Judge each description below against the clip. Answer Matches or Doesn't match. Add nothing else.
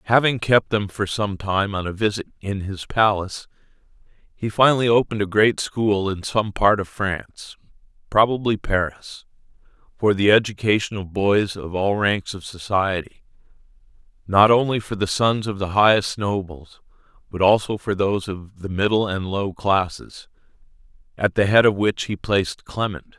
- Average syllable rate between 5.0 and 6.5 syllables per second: Doesn't match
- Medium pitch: Doesn't match